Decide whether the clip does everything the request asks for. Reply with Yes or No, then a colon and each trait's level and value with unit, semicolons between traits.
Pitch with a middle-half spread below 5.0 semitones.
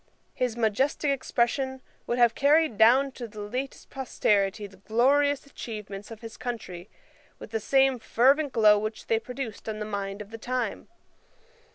Yes: average, 4.0 semitones